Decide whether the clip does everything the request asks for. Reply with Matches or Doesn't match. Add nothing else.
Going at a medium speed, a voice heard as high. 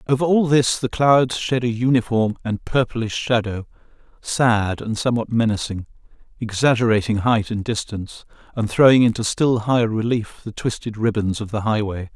Doesn't match